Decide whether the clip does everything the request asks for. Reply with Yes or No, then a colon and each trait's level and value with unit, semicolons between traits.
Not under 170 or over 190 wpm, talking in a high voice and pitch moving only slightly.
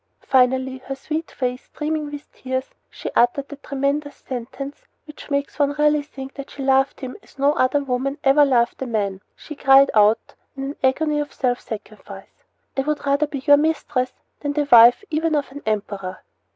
Yes: average, 185 wpm; very high, 275 Hz; narrow, 2.3 semitones